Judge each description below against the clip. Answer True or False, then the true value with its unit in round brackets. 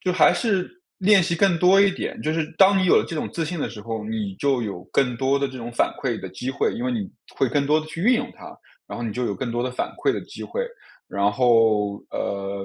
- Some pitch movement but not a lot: False (8.0 semitones)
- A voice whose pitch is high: False (135 Hz)